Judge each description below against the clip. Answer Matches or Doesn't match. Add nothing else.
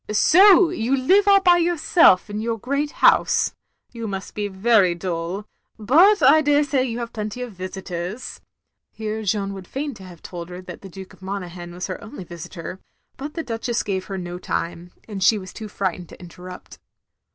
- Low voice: Doesn't match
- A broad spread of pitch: Matches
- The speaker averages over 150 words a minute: Matches